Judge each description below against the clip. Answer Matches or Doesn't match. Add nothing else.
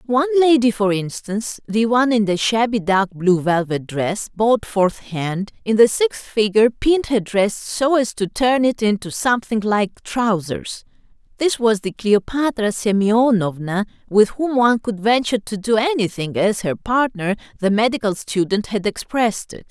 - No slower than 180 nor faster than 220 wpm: Doesn't match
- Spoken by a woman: Matches